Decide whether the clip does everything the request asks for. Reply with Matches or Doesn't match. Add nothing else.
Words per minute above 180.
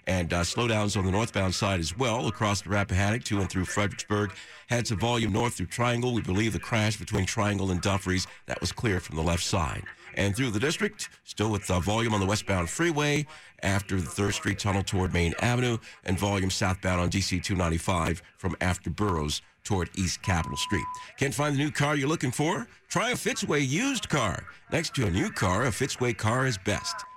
Matches